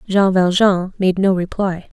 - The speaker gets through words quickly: No, average, 150 wpm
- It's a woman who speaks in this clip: Yes, female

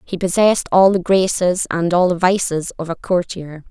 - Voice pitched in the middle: Yes, medium, 180 Hz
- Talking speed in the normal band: Yes, average, 195 wpm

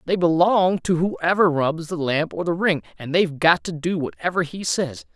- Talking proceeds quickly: Yes, fast, 210 wpm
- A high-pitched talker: No, medium, 165 Hz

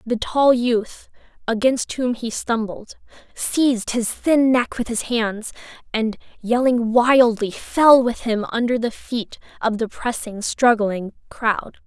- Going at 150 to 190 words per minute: No, average, 140 wpm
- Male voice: No, female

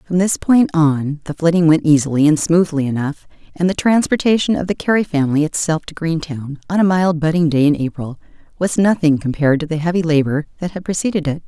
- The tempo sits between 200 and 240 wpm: Yes, fast, 205 wpm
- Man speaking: No, female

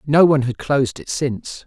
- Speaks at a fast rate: Yes, fast, 215 wpm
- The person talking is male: Yes, male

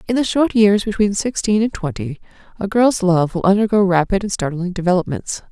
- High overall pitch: Yes, high, 200 Hz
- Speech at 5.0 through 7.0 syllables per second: Yes, 5.5 syllables/s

